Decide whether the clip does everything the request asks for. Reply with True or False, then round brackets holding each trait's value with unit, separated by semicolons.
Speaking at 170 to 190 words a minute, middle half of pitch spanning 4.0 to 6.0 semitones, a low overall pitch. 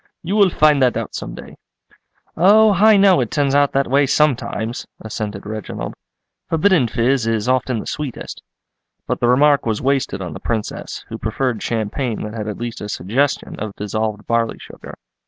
True (175 wpm; 4.9 semitones; 125 Hz)